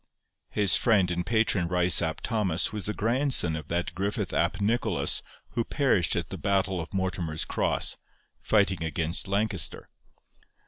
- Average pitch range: Yes, average, 3.8 semitones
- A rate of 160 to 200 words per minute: No, average, 145 wpm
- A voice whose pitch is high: No, very low, 95 Hz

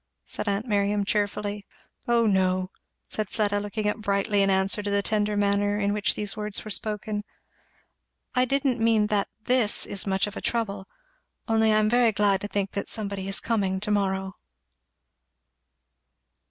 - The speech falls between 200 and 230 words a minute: No, average, 170 wpm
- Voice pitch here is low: No, high, 205 Hz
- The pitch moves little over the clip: Yes, narrow, 1.4 semitones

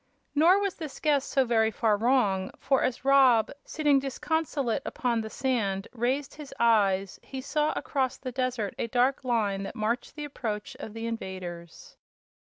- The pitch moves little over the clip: No, average, 4.1 semitones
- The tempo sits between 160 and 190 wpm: Yes, average, 165 wpm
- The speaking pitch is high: Yes, high, 245 Hz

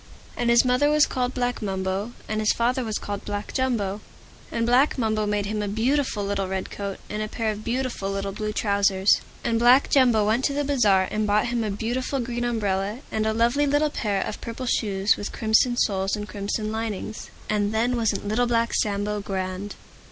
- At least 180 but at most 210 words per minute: Yes, average, 200 wpm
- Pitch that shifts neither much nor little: Yes, average, 3.0 semitones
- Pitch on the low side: No, high, 215 Hz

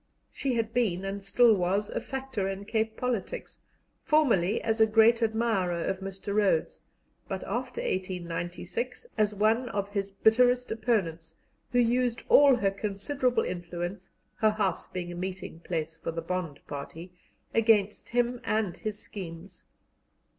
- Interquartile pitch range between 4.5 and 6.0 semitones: No, average, 4.0 semitones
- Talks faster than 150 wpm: No, average, 145 wpm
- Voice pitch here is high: Yes, high, 205 Hz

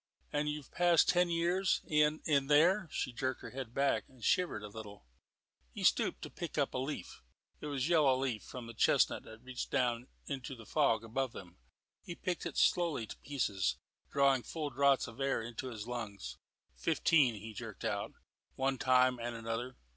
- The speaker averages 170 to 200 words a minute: Yes, average, 185 wpm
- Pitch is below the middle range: Yes, low, 130 Hz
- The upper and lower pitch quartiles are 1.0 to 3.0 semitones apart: No, average, 4.6 semitones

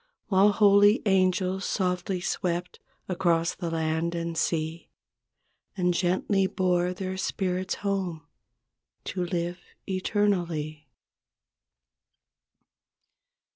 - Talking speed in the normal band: No, slow, 85 wpm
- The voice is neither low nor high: Yes, medium, 180 Hz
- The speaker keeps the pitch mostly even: Yes, narrow, 2.1 semitones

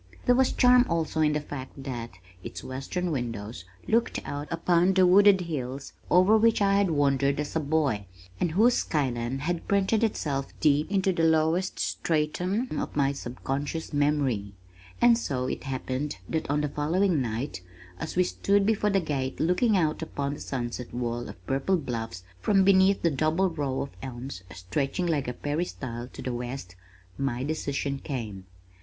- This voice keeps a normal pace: Yes, average, 170 wpm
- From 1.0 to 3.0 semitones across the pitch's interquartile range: No, wide, 5.5 semitones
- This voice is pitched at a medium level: Yes, medium, 150 Hz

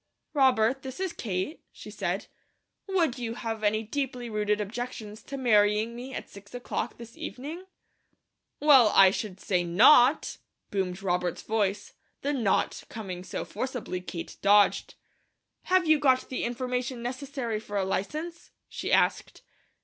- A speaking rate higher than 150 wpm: No, average, 140 wpm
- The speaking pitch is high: Yes, high, 235 Hz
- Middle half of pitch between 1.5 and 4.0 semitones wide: No, average, 4.4 semitones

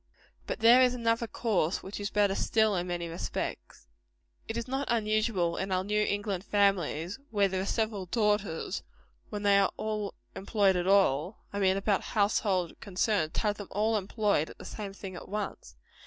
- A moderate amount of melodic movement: No, narrow, 2.3 semitones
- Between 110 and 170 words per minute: No, average, 180 wpm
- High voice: Yes, high, 205 Hz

